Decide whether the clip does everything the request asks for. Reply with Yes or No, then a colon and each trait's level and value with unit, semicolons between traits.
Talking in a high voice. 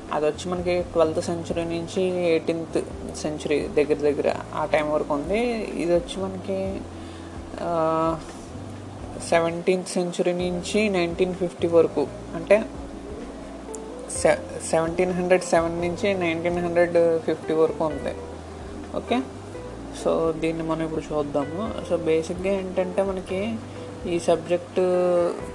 No: medium, 170 Hz